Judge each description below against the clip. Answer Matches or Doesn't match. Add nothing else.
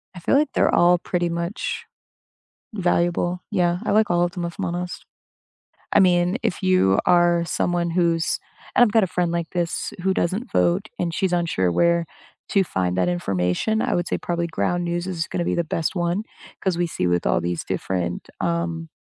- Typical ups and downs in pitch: Doesn't match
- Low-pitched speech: Doesn't match